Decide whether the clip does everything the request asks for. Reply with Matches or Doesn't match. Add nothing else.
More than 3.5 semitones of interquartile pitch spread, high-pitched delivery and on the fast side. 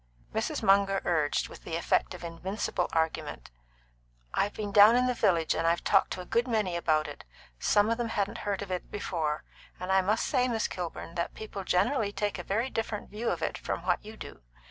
Matches